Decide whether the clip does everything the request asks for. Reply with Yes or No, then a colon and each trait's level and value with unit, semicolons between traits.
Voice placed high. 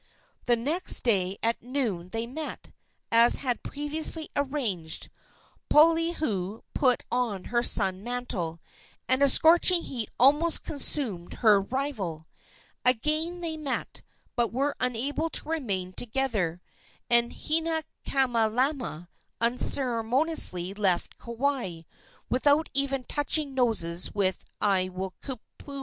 Yes: high, 245 Hz